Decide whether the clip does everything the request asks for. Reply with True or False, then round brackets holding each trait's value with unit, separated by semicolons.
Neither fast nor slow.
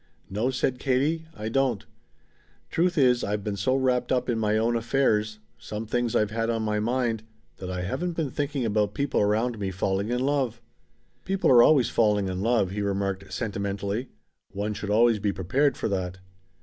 True (185 wpm)